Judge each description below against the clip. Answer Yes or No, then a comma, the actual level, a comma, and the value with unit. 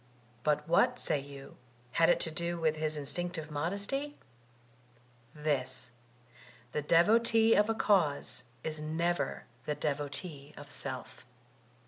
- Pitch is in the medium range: Yes, medium, 155 Hz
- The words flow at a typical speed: No, slow, 120 wpm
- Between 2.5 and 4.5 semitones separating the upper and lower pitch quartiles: Yes, average, 3.4 semitones